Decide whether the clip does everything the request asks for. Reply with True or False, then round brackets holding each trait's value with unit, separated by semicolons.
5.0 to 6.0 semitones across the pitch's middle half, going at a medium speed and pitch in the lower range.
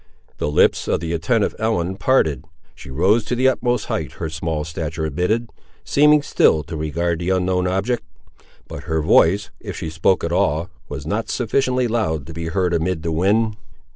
True (5.5 semitones; 180 wpm; 90 Hz)